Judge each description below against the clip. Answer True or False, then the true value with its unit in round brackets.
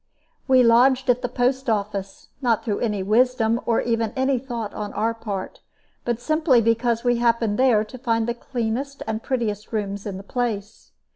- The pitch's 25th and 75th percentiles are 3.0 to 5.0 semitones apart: False (2.6 semitones)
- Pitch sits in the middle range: False (230 Hz)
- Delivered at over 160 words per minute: True (180 wpm)